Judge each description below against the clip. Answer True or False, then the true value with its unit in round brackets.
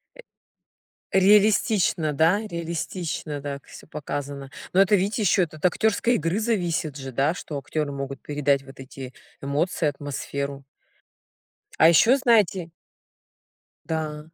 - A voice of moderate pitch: True (155 Hz)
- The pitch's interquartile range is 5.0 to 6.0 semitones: True (5.3 semitones)